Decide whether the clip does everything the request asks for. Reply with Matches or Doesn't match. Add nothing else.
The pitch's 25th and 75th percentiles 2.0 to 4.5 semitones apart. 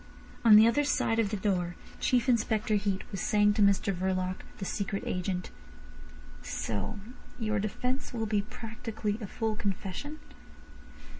Matches